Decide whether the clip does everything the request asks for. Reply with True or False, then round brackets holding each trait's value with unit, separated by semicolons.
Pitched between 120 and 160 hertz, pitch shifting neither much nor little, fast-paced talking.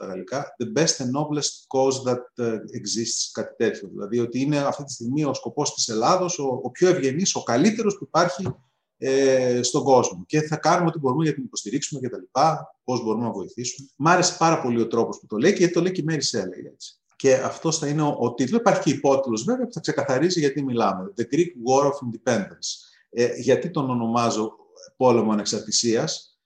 True (135 Hz; 4.9 semitones; 210 wpm)